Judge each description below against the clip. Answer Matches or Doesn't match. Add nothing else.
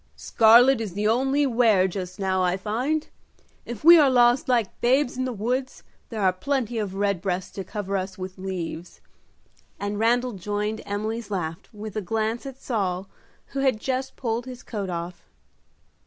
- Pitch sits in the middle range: Doesn't match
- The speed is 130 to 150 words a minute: Doesn't match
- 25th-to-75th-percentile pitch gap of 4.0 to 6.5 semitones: Matches